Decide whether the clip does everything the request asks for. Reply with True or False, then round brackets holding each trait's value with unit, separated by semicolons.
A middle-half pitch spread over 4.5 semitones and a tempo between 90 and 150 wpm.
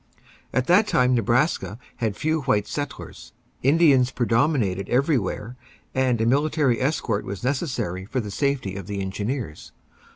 True (5.3 semitones; 135 wpm)